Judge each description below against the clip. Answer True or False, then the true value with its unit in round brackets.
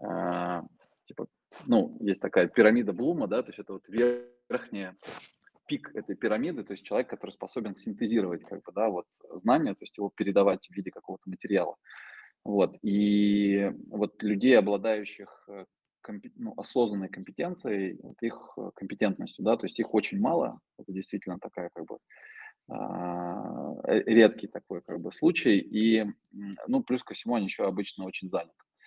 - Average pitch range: True (3.6 semitones)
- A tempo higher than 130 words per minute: True (155 wpm)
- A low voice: True (105 Hz)